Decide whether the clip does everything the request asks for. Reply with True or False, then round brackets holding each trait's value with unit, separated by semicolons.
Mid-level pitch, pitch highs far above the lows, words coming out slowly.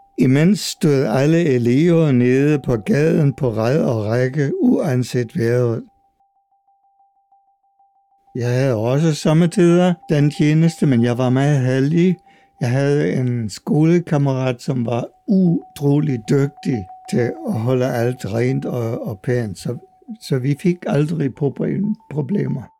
True (145 Hz; 7.0 semitones; 115 wpm)